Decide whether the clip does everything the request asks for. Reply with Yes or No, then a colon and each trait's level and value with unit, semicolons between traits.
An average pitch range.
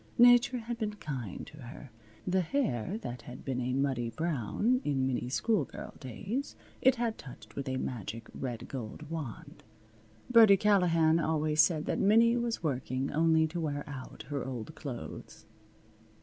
No: wide, 8.0 semitones